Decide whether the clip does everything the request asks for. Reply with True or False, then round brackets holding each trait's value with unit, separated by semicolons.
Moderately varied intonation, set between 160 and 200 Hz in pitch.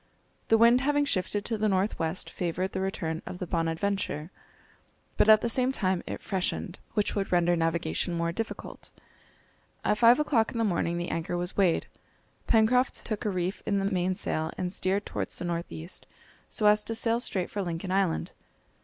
True (3.8 semitones; 190 Hz)